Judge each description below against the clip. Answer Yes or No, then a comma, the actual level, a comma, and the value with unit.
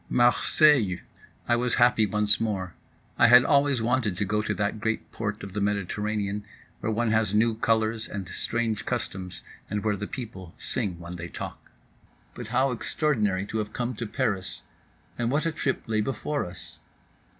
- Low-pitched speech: Yes, low, 110 Hz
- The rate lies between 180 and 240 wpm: No, average, 170 wpm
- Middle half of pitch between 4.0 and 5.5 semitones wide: No, average, 2.9 semitones